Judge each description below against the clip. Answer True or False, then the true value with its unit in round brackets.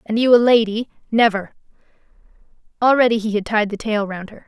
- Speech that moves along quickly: False (175 wpm)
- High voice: True (220 Hz)